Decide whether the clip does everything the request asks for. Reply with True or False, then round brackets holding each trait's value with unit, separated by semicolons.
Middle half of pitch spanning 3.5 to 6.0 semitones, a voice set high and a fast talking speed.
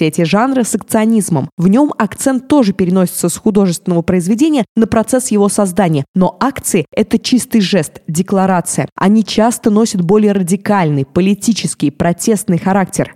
False (3.9 semitones; 200 Hz; 135 wpm)